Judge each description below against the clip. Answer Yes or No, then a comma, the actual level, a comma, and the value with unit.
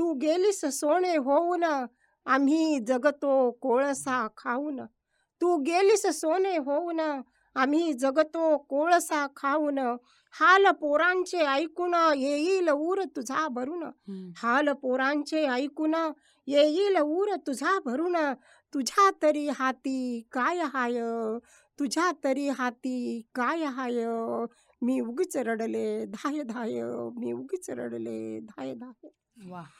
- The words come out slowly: No, average, 105 wpm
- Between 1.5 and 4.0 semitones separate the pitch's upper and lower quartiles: No, average, 4.4 semitones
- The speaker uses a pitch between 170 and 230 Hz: No, very high, 285 Hz